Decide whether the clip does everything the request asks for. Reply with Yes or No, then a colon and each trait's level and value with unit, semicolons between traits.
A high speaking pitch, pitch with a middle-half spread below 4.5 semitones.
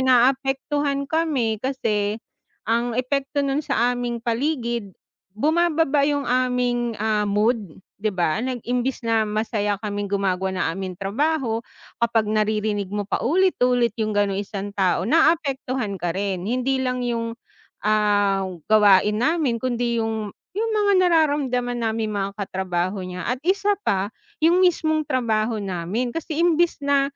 No: high, 235 Hz; average, 4.9 semitones